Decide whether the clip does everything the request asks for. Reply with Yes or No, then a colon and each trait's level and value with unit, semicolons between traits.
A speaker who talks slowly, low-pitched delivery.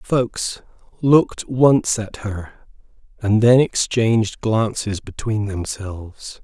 Yes: slow, 105 wpm; low, 110 Hz